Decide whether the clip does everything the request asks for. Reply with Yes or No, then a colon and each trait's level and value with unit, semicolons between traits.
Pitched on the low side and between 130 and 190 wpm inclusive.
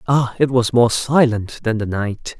No: low, 120 Hz; average, 200 wpm